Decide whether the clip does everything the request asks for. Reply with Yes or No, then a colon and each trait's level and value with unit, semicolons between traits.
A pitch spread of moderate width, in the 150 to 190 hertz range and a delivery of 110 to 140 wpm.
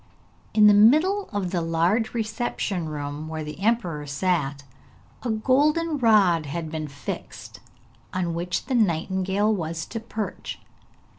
No: wide, 5.7 semitones; medium, 185 Hz; slow, 135 wpm